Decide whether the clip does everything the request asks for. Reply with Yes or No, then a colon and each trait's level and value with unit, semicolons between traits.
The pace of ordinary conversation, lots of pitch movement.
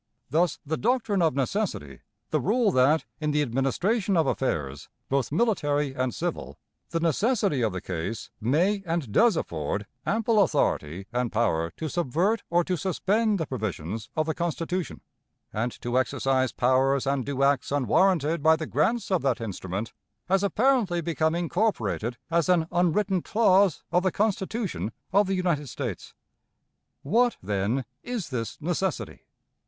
Yes: average, 150 wpm; wide, 7.3 semitones